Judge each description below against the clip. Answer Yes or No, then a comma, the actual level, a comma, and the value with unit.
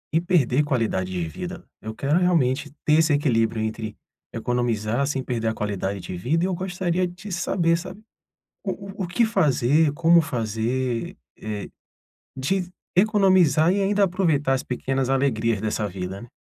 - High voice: No, medium, 140 Hz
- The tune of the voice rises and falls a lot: Yes, wide, 7.6 semitones